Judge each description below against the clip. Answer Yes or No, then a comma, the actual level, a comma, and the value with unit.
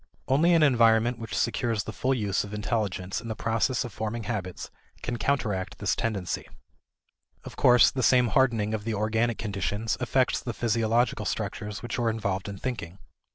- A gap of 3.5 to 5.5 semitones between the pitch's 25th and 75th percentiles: No, average, 2.7 semitones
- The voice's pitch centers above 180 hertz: No, low, 115 Hz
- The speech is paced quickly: No, average, 170 wpm